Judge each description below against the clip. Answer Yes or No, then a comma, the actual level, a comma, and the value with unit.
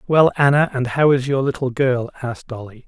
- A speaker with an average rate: No, fast, 210 wpm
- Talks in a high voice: No, low, 130 Hz